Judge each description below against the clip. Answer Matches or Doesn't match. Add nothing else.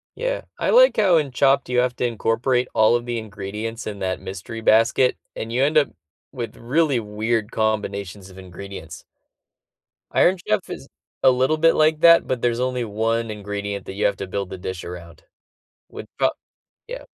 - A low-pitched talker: Matches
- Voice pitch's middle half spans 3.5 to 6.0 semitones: Matches